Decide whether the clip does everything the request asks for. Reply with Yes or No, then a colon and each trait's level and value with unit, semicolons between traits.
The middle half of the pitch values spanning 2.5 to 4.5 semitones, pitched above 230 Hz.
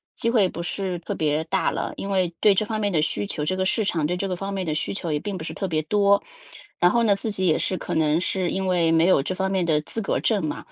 No: average, 3.4 semitones; medium, 185 Hz